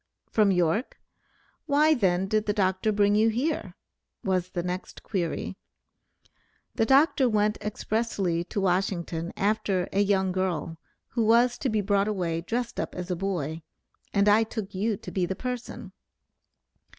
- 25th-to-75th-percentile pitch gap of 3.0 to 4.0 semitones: Yes, average, 3.3 semitones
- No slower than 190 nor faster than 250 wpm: No, average, 150 wpm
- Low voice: No, high, 200 Hz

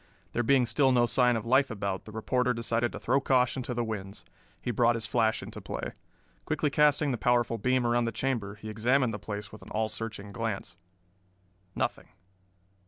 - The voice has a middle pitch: No, low, 120 Hz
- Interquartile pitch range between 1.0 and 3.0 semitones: Yes, narrow, 2.6 semitones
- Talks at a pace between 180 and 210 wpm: Yes, average, 190 wpm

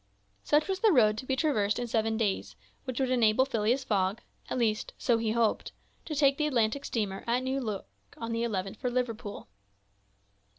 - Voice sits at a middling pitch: No, high, 235 Hz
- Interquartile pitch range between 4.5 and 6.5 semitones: No, average, 3.5 semitones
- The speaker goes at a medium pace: Yes, average, 175 wpm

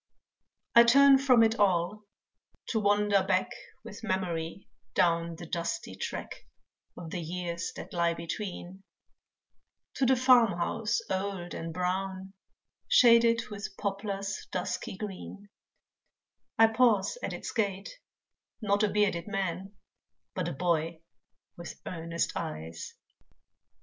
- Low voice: No, high, 195 Hz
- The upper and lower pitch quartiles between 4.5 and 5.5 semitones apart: No, average, 3.7 semitones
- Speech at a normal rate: No, slow, 120 wpm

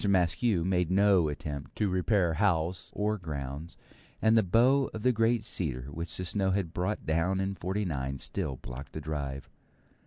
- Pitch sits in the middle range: No, very low, 90 Hz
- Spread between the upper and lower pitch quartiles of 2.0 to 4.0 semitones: No, average, 4.8 semitones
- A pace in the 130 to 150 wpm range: No, average, 165 wpm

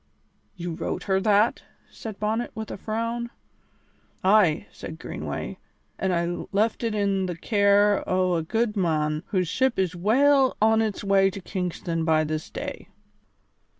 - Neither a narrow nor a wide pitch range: Yes, average, 3.8 semitones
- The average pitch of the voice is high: Yes, high, 200 Hz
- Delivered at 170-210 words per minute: No, average, 150 wpm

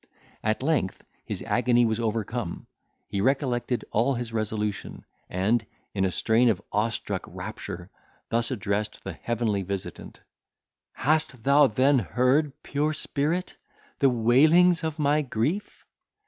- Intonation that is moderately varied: Yes, average, 4.7 semitones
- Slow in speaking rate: Yes, slow, 125 wpm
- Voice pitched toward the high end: No, low, 120 Hz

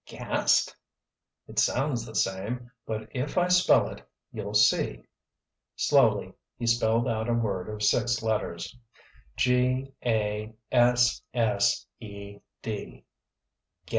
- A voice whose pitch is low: Yes, low, 115 Hz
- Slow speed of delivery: Yes, slow, 110 wpm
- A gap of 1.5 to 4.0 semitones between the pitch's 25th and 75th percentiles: Yes, narrow, 2.5 semitones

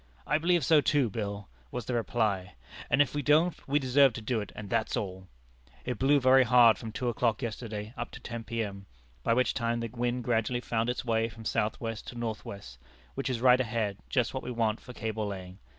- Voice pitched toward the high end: No, low, 115 Hz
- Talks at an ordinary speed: No, fast, 220 wpm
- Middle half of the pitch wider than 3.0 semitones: No, average, 2.7 semitones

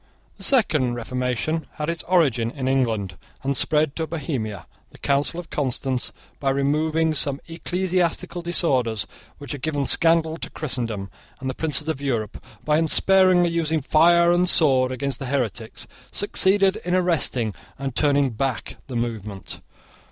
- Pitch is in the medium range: Yes, medium, 145 Hz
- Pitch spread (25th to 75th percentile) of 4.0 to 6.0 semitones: Yes, average, 4.6 semitones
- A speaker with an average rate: Yes, average, 145 wpm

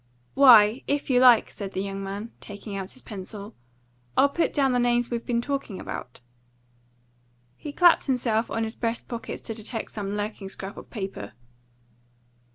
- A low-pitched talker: No, high, 225 Hz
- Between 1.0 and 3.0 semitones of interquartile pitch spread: No, average, 3.7 semitones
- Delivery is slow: No, average, 165 wpm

